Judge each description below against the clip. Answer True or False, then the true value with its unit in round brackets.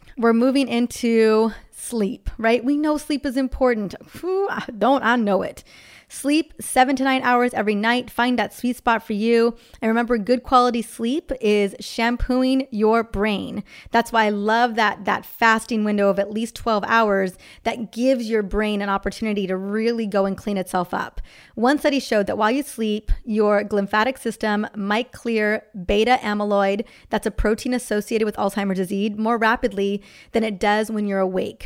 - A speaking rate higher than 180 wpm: False (175 wpm)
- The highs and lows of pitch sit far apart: False (2.7 semitones)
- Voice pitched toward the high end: True (225 Hz)